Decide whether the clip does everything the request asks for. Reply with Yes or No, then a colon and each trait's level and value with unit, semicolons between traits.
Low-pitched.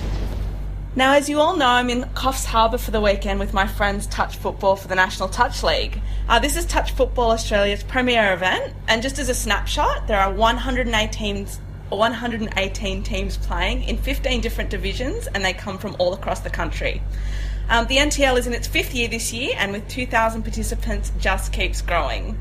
No: high, 225 Hz